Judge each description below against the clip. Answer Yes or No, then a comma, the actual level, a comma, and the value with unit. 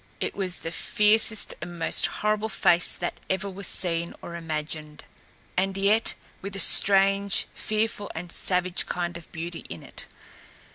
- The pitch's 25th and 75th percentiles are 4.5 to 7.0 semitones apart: No, average, 2.8 semitones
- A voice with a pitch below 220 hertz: Yes, medium, 185 Hz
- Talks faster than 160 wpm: No, average, 150 wpm